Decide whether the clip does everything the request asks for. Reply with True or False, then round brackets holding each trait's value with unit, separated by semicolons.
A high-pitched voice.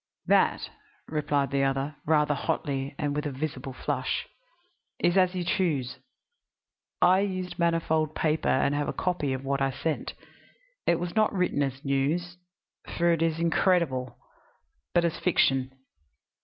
False (155 Hz)